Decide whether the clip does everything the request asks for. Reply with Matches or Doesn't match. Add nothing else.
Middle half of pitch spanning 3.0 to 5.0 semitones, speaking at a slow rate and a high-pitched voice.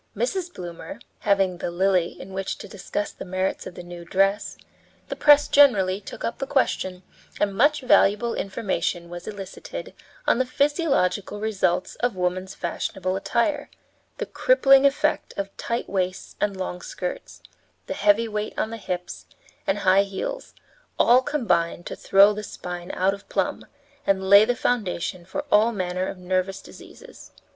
Doesn't match